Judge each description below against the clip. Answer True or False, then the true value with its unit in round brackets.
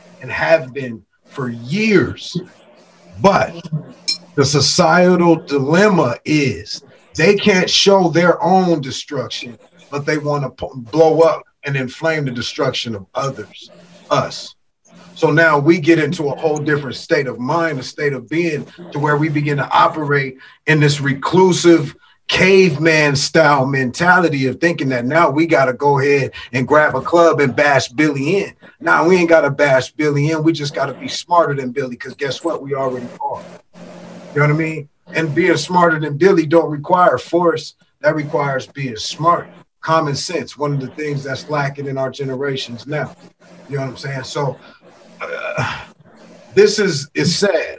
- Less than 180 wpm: True (170 wpm)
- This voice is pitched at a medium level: True (150 Hz)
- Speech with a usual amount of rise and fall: True (3.4 semitones)